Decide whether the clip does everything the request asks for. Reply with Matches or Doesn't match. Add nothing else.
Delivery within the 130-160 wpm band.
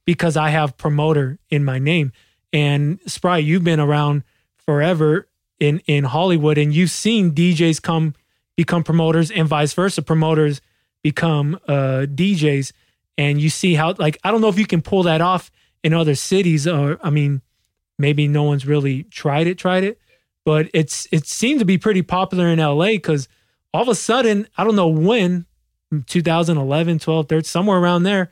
Doesn't match